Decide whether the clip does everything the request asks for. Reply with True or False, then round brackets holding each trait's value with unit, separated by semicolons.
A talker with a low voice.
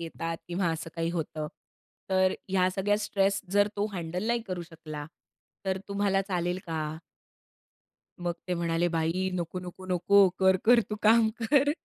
False (185 Hz)